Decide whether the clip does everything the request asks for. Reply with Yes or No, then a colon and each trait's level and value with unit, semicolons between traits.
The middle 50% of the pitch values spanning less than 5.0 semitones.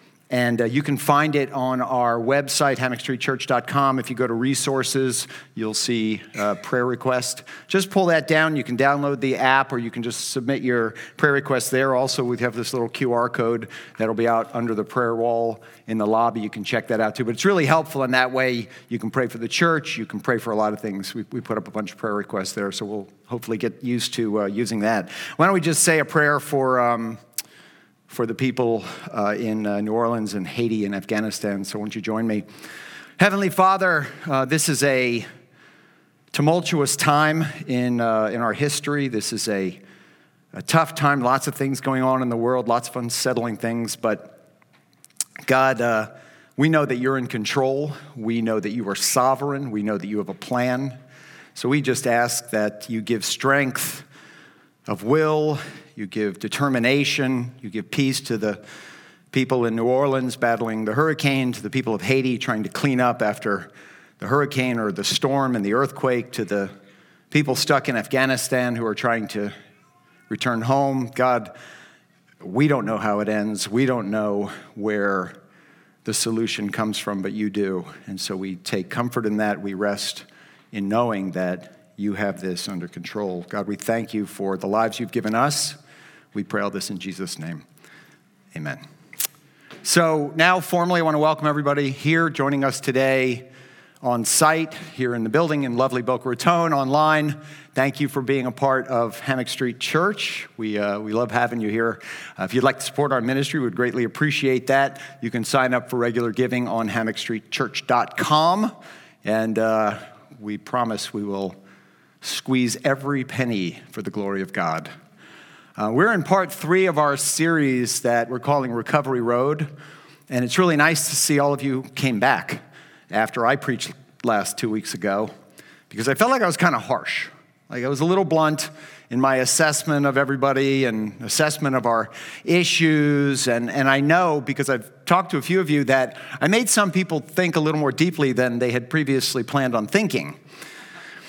Yes: average, 4.2 semitones